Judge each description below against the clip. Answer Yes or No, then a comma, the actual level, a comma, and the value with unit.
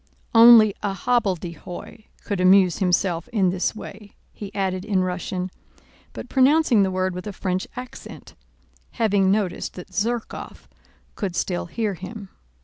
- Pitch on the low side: No, high, 195 Hz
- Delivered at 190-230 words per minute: No, slow, 135 wpm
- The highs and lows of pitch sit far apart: No, average, 2.9 semitones